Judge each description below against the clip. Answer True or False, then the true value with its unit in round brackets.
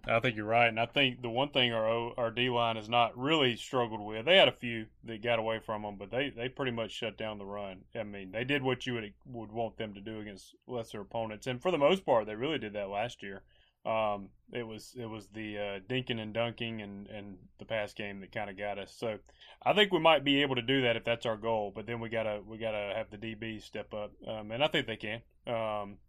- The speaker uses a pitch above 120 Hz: False (115 Hz)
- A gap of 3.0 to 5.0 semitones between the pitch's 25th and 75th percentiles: False (2.4 semitones)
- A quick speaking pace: True (265 wpm)